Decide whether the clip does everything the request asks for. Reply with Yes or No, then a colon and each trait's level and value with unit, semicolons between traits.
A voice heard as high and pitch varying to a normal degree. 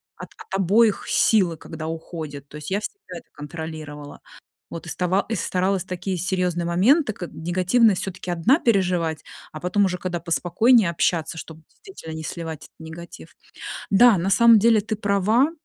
No: medium, 180 Hz; average, 3.9 semitones